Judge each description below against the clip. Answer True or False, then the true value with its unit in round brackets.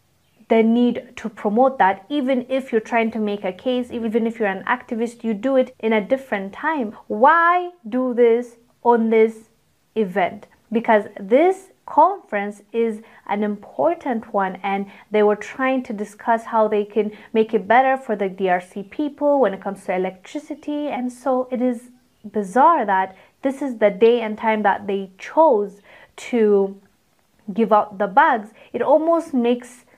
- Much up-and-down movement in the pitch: False (3.7 semitones)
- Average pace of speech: True (165 wpm)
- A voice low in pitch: False (230 Hz)